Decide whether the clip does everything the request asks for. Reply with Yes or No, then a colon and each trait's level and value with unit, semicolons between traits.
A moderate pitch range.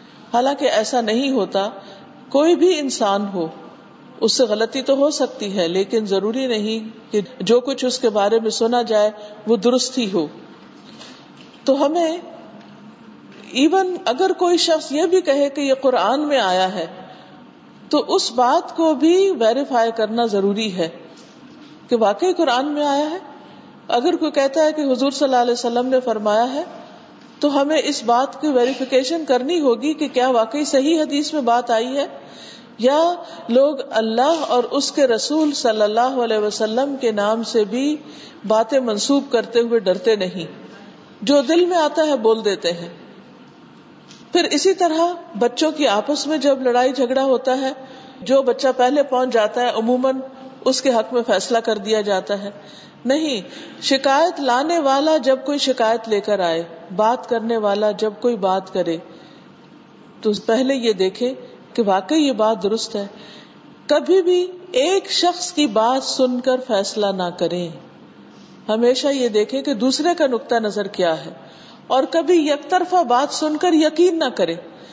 Yes: average, 4.8 semitones